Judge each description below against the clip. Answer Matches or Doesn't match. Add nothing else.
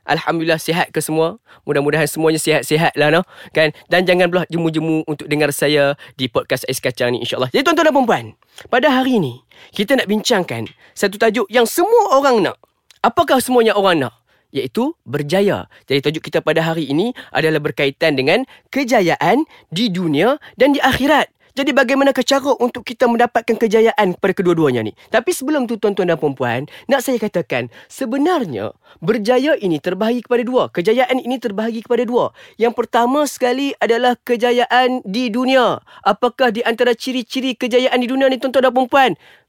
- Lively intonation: Matches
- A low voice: Doesn't match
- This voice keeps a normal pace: Doesn't match